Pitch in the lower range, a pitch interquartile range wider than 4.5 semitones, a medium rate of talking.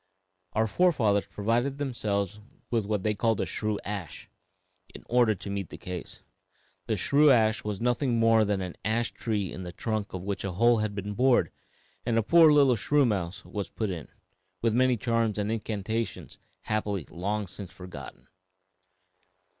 No: low, 110 Hz; average, 2.8 semitones; average, 165 wpm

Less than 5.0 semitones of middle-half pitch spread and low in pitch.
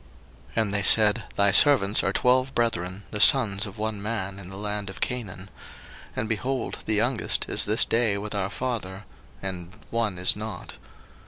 Yes: average, 2.8 semitones; low, 105 Hz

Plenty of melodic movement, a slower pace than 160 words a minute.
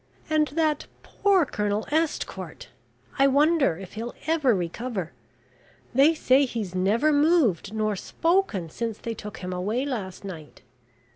Yes: wide, 7.5 semitones; slow, 135 wpm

